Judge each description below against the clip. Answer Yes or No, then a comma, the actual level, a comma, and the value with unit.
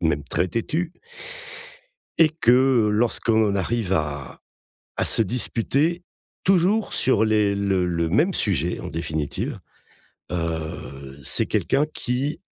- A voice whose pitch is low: Yes, low, 105 Hz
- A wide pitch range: Yes, wide, 8.3 semitones